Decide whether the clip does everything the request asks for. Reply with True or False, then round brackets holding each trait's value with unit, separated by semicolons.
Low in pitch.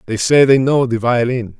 True (125 Hz)